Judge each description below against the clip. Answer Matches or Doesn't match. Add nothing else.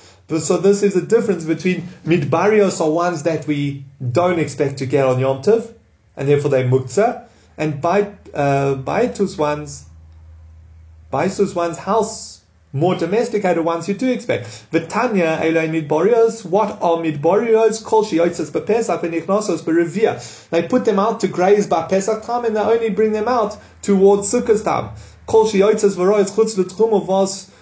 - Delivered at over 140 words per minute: Doesn't match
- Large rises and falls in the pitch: Matches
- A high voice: Doesn't match